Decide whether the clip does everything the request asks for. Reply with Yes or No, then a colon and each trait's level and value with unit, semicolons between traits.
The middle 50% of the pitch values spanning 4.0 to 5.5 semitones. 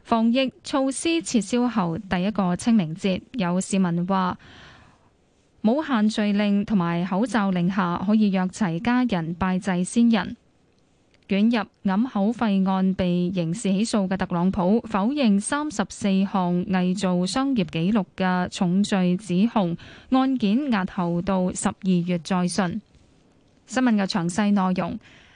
No: average, 3.5 semitones